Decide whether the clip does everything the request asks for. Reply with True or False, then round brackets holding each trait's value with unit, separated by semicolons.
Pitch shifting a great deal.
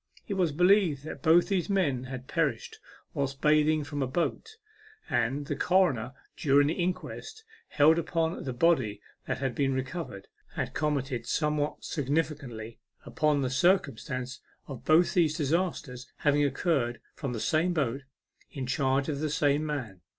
False (3.9 semitones)